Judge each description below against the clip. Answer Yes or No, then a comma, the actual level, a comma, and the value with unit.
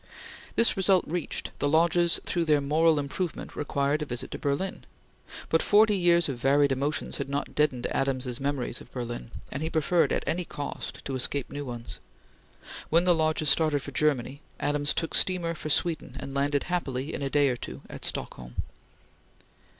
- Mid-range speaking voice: Yes, medium, 145 Hz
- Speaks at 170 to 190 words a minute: Yes, average, 175 wpm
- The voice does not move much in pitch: No, average, 3.4 semitones